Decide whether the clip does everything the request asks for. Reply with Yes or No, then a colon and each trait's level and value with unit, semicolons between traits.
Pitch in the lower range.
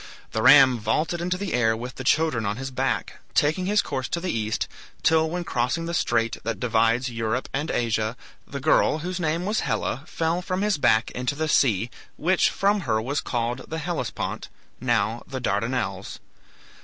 Yes: low, 130 Hz